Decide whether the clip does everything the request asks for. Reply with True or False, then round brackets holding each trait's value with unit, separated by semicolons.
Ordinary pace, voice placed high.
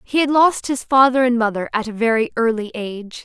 False (220 wpm; 240 Hz)